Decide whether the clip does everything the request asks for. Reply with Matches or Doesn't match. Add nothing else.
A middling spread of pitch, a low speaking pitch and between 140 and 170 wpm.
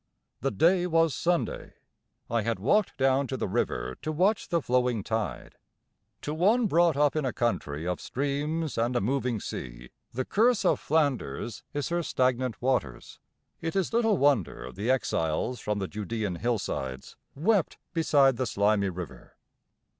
Doesn't match